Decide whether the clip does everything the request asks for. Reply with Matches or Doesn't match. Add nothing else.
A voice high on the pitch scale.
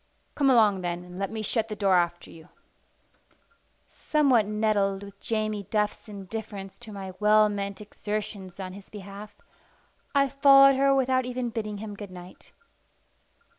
Matches